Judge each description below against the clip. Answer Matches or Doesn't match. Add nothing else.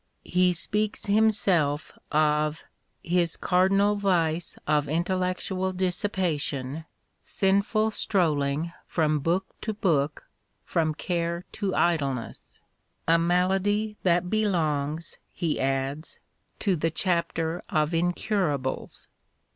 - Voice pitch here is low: Doesn't match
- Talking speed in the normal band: Doesn't match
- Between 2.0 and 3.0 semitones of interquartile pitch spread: Doesn't match